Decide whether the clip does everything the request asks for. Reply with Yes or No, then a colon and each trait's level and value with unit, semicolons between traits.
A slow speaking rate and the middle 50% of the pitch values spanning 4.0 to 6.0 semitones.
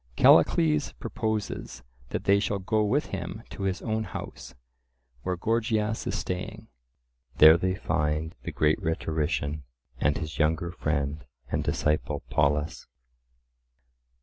Yes: slow, 120 wpm; average, 4.9 semitones